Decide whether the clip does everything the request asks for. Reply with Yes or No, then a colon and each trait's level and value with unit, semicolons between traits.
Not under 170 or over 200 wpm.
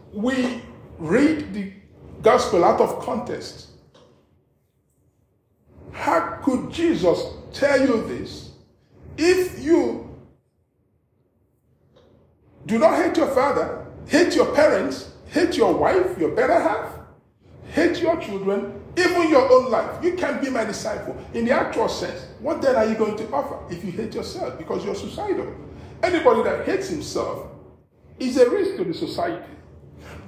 No: slow, 135 wpm